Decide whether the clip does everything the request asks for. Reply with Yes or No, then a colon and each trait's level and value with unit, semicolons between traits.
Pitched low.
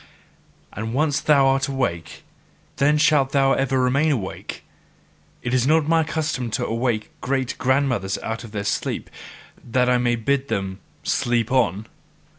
Yes: low, 130 Hz